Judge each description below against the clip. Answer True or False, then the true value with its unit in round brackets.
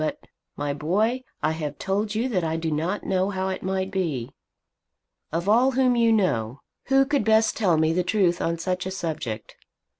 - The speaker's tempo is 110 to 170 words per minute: False (190 wpm)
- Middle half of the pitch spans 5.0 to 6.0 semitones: True (5.3 semitones)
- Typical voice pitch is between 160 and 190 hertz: True (185 Hz)